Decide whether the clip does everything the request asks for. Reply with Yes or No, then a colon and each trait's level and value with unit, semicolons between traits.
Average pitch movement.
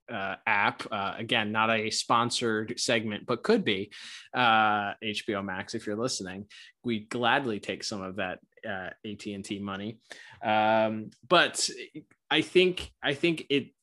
No: narrow, 2.1 semitones